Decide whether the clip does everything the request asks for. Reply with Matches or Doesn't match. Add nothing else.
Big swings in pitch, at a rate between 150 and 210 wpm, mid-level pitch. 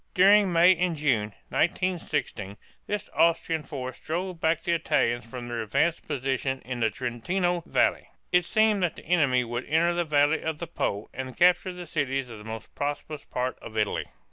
Matches